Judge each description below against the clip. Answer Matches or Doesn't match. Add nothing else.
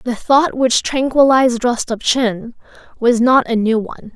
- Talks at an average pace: Matches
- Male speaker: Doesn't match